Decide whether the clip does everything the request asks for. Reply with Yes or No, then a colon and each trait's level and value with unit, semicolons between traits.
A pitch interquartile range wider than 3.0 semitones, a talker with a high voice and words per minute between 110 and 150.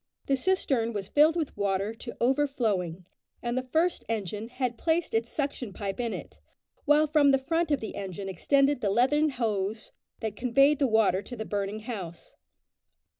No: wide, 5.5 semitones; high, 240 Hz; average, 175 wpm